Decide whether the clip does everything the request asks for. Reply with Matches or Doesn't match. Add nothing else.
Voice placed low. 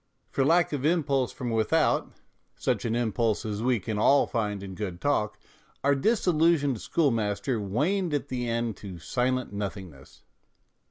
Matches